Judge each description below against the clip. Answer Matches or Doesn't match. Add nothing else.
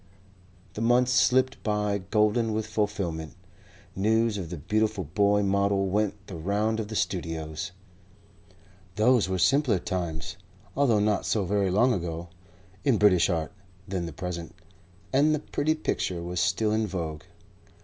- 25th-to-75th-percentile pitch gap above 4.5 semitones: Doesn't match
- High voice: Doesn't match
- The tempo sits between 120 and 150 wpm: Matches